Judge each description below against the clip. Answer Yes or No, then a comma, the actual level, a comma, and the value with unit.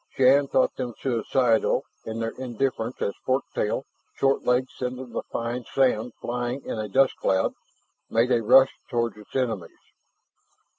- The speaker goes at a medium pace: Yes, average, 150 wpm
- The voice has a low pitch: Yes, low, 125 Hz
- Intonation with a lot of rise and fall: No, narrow, 2.5 semitones